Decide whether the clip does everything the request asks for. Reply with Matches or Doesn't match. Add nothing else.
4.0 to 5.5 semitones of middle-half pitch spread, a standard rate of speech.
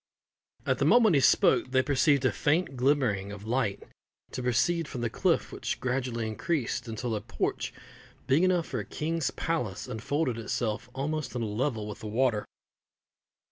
Matches